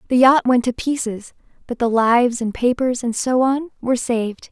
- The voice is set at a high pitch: Yes, high, 245 Hz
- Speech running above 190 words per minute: Yes, average, 200 wpm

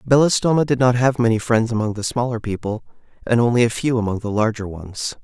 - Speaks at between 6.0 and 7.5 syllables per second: Yes, 6.1 syllables/s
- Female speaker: No, male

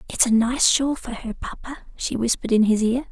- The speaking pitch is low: No, high, 240 Hz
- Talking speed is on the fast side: Yes, fast, 230 wpm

